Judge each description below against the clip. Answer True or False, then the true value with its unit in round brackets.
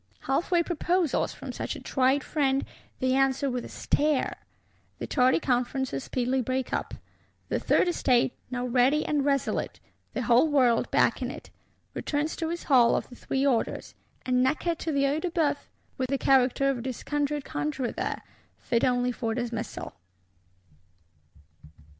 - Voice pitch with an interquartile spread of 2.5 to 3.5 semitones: True (2.8 semitones)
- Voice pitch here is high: True (265 Hz)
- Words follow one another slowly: False (155 wpm)